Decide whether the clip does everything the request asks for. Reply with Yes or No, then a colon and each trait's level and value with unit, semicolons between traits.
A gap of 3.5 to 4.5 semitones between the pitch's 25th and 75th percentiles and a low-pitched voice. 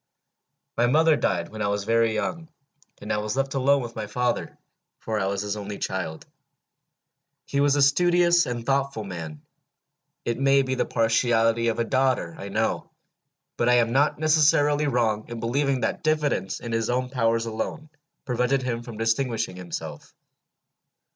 Yes: average, 4.0 semitones; low, 120 Hz